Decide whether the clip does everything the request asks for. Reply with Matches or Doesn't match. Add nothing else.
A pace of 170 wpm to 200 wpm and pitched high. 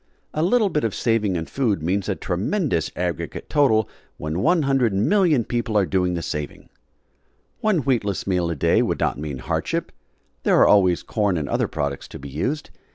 Doesn't match